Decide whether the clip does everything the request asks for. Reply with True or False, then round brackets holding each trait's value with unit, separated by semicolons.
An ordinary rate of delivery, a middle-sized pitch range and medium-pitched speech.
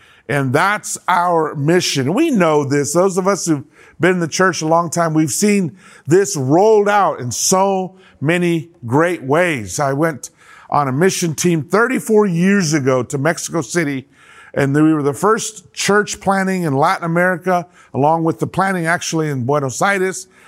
True (170 wpm; 4.2 semitones; 170 Hz)